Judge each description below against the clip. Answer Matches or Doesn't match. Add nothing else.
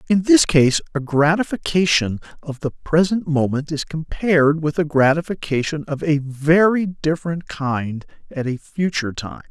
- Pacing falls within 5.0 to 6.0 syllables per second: Doesn't match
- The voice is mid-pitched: Matches